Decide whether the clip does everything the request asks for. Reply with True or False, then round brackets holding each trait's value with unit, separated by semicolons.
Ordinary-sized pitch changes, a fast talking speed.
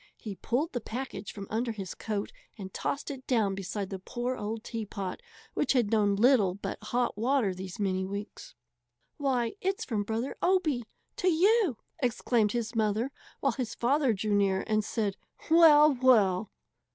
False (4.3 semitones; 165 wpm)